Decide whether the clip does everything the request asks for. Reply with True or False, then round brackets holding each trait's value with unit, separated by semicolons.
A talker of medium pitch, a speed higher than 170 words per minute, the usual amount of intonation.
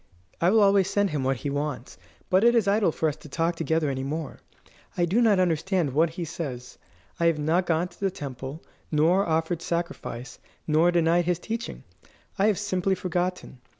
True (170 Hz; 190 wpm; 3.6 semitones)